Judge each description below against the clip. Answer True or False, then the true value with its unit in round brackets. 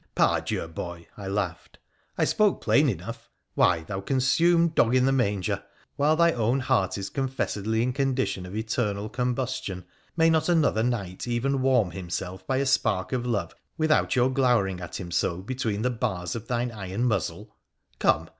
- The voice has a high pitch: False (120 Hz)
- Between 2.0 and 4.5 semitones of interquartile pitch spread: False (5.4 semitones)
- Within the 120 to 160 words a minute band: False (185 wpm)